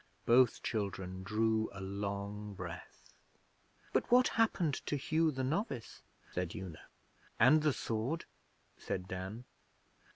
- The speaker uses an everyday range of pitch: No, wide, 6.5 semitones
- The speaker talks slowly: Yes, slow, 120 wpm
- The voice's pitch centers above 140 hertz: No, low, 110 Hz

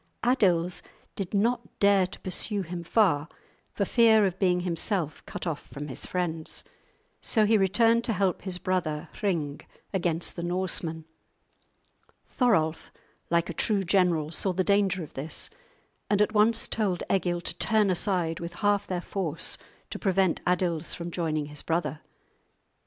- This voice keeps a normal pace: Yes, average, 150 wpm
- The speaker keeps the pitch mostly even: No, average, 3.3 semitones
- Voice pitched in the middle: Yes, medium, 180 Hz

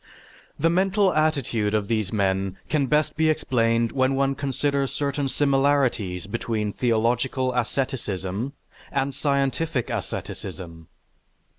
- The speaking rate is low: Yes, slow, 110 wpm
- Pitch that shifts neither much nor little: Yes, average, 4.5 semitones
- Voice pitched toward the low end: Yes, low, 130 Hz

